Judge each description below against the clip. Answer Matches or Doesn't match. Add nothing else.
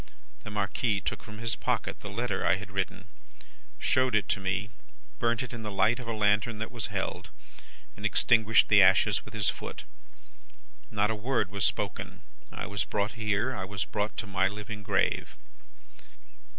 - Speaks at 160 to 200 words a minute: Matches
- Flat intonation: Matches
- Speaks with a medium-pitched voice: Doesn't match